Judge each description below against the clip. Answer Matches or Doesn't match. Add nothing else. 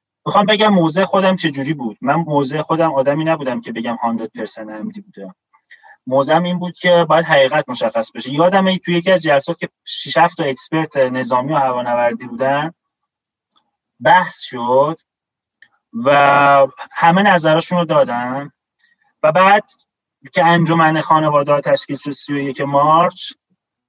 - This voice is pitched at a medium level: Matches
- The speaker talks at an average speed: Matches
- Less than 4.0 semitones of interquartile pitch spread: Doesn't match